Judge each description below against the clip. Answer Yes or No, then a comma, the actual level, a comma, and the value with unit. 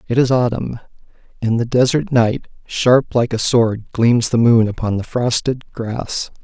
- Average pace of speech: Yes, average, 170 wpm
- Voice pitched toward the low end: Yes, low, 115 Hz